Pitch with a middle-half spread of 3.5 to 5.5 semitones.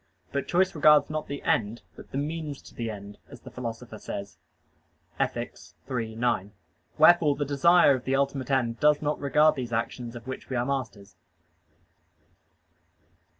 Yes: average, 4.2 semitones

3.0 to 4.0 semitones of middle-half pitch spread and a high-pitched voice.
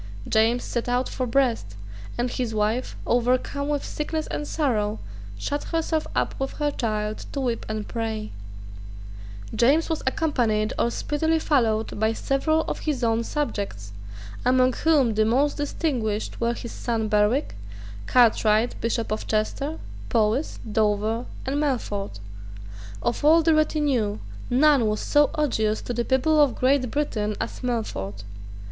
No: average, 4.9 semitones; high, 245 Hz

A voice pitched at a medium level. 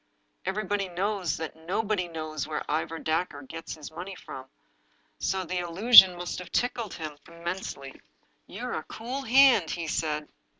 Yes: medium, 175 Hz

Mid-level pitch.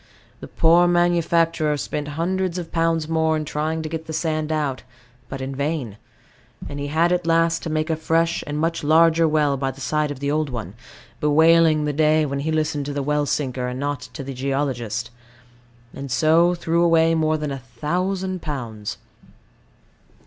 Yes: medium, 155 Hz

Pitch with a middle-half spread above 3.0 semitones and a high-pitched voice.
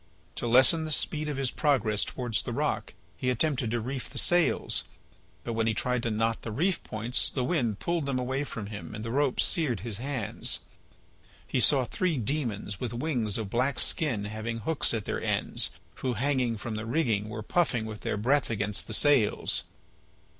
No: average, 4.4 semitones; low, 120 Hz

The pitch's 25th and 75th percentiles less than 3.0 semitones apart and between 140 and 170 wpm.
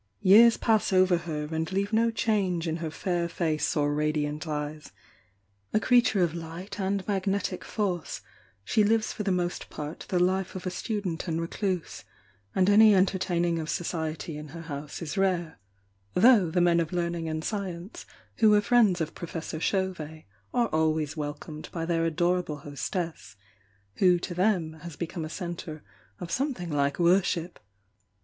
No: average, 3.4 semitones; average, 165 wpm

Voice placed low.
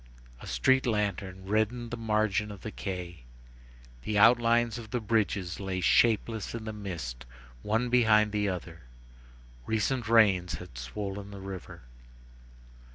Yes: low, 105 Hz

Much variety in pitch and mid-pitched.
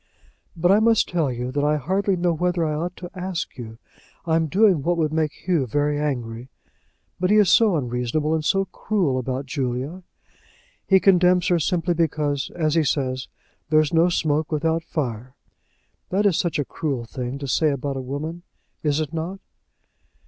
No: average, 4.3 semitones; medium, 155 Hz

